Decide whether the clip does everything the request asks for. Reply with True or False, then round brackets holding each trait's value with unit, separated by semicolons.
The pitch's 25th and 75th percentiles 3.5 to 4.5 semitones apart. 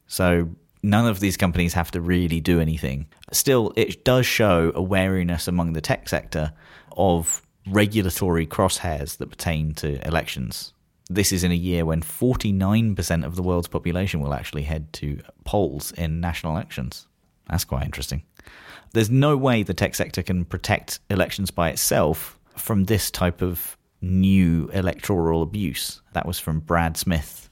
False (2.9 semitones)